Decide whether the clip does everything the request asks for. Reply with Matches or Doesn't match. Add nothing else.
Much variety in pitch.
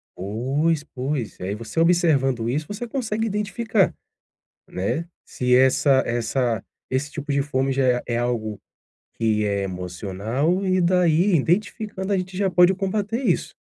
Matches